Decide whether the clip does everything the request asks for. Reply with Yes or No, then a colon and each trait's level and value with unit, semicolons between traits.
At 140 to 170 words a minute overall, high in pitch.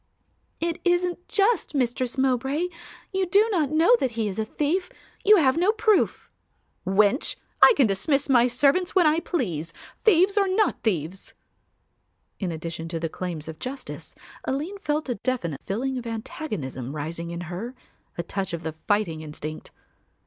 Yes: average, 160 wpm; very high, 255 Hz